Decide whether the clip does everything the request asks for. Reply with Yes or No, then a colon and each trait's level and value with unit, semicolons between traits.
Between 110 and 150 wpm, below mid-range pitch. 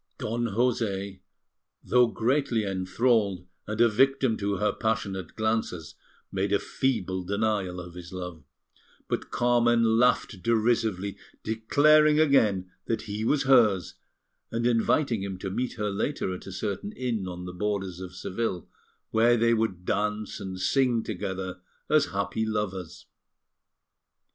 Yes: slow, 135 wpm; low, 105 Hz